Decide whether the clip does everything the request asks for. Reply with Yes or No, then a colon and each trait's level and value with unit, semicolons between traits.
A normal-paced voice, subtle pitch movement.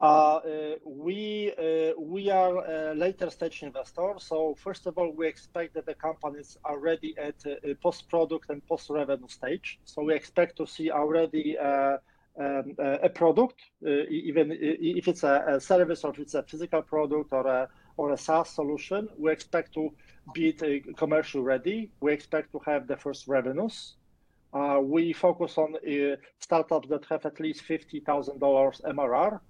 Yes: average, 175 wpm; narrow, 2.2 semitones